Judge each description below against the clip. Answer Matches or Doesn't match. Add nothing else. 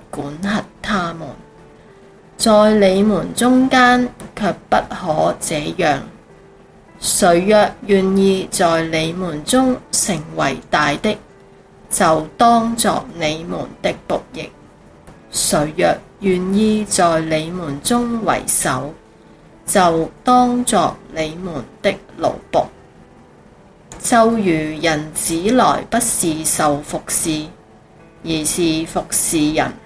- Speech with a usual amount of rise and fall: Doesn't match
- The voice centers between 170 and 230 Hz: Matches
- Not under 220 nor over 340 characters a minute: Doesn't match